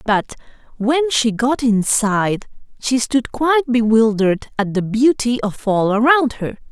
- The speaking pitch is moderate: No, high, 235 Hz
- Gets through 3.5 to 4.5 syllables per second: Yes, 4.3 syllables/s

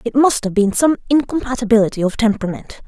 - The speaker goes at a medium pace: Yes, average, 165 wpm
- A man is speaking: No, female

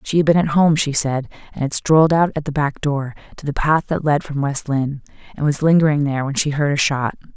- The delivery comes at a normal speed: No, fast, 260 wpm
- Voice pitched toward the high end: No, medium, 145 Hz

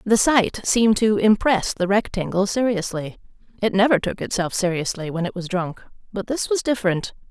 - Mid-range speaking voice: No, high, 205 Hz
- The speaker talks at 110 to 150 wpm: No, average, 170 wpm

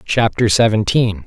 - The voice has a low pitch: Yes, low, 105 Hz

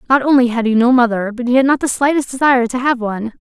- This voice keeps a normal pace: No, fast, 280 wpm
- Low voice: No, very high, 250 Hz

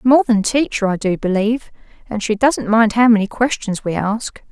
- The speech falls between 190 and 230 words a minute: Yes, average, 200 wpm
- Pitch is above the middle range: Yes, high, 220 Hz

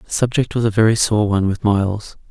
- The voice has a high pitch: No, low, 105 Hz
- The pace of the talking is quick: Yes, fast, 235 wpm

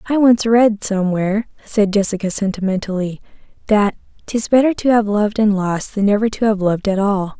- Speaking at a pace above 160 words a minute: Yes, average, 180 wpm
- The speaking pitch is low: No, high, 205 Hz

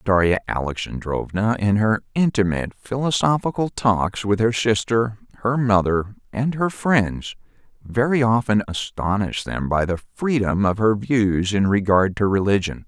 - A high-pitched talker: No, low, 105 Hz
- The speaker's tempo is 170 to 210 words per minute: No, slow, 135 wpm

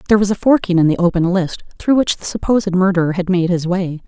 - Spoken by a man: No, female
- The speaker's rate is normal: No, fast, 250 wpm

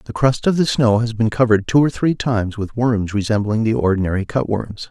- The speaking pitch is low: Yes, low, 115 Hz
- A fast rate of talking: Yes, fast, 230 wpm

